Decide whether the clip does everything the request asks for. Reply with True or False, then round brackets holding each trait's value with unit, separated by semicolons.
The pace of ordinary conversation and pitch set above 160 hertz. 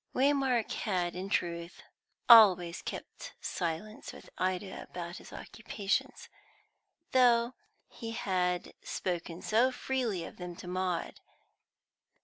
False (110 wpm; 190 Hz)